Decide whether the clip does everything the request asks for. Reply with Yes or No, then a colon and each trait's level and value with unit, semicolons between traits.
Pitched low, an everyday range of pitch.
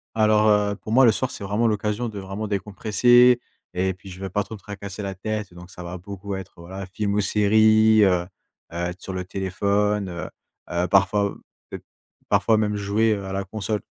No: low, 100 Hz; narrow, 2.1 semitones